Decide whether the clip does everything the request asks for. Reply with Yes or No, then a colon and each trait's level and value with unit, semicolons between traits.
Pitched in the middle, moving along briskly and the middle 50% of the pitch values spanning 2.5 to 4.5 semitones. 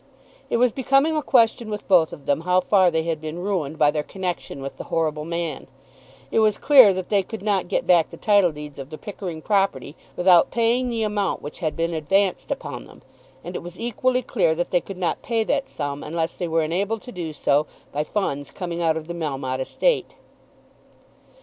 No: medium, 175 Hz; fast, 210 wpm; average, 5.0 semitones